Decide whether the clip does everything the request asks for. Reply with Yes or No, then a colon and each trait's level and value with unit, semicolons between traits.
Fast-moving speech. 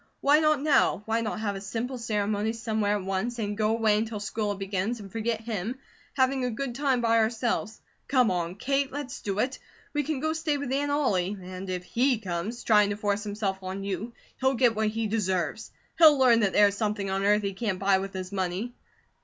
Yes: fast, 215 wpm